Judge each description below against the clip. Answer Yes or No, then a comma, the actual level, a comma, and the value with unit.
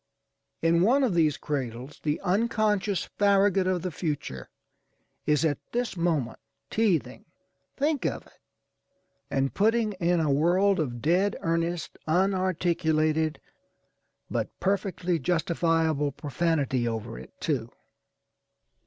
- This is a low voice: No, medium, 170 Hz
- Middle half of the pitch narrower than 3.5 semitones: No, average, 4.5 semitones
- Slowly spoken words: Yes, slow, 110 wpm